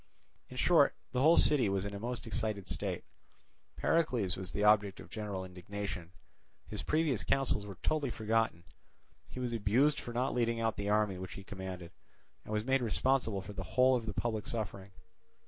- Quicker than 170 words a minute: Yes, average, 180 wpm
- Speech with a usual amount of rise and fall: Yes, average, 3.8 semitones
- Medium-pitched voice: No, low, 110 Hz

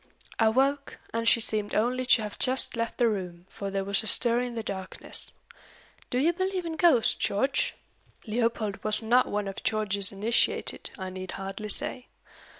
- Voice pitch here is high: Yes, high, 225 Hz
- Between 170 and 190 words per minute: Yes, average, 175 wpm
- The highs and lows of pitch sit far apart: No, average, 3.8 semitones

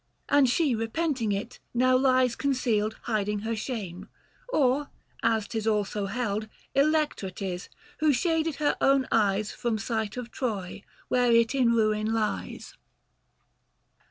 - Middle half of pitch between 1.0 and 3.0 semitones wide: No, average, 3.6 semitones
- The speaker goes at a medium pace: No, slow, 130 wpm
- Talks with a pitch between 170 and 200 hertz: No, high, 230 Hz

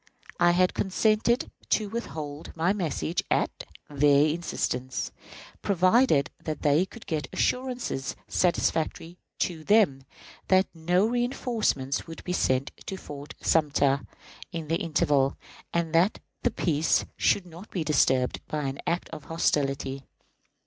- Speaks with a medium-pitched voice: Yes, medium, 165 Hz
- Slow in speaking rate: Yes, slow, 125 wpm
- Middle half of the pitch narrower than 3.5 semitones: No, average, 4.7 semitones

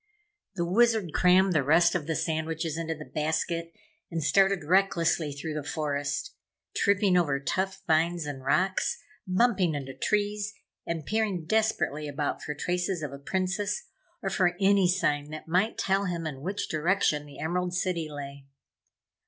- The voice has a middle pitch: Yes, medium, 170 Hz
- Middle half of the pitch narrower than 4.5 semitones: Yes, average, 4.0 semitones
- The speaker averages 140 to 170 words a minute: Yes, average, 155 wpm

